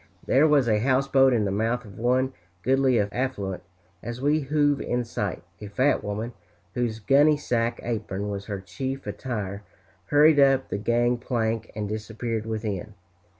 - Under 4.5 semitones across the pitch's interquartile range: Yes, average, 4.0 semitones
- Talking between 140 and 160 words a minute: Yes, average, 155 wpm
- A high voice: No, low, 120 Hz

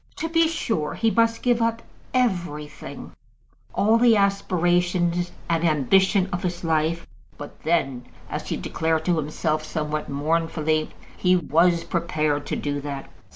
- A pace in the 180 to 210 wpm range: No, average, 140 wpm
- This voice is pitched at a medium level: Yes, medium, 170 Hz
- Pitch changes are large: No, average, 3.9 semitones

